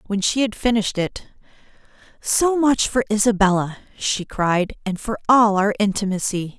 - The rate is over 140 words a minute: No, slow, 135 wpm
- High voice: Yes, high, 210 Hz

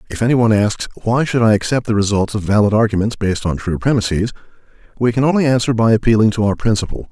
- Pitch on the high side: No, low, 110 Hz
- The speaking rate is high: Yes, fast, 220 wpm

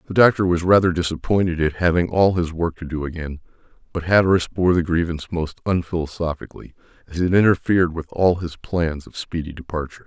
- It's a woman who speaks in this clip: No, male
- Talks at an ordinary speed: Yes, average, 180 wpm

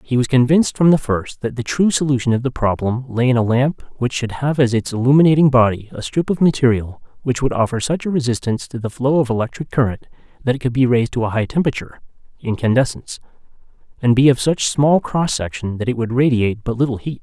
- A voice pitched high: No, low, 125 Hz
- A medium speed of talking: No, fast, 215 wpm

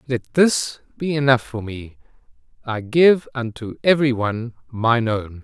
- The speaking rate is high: No, average, 145 wpm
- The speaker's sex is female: No, male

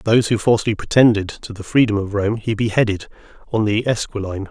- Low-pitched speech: Yes, low, 105 Hz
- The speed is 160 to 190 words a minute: Yes, average, 185 wpm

